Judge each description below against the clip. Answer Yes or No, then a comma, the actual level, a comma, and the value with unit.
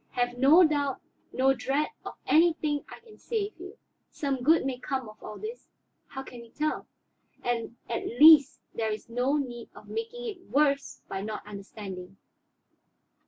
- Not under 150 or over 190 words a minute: Yes, average, 165 wpm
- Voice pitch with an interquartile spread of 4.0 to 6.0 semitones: Yes, average, 5.1 semitones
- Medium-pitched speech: No, very high, 270 Hz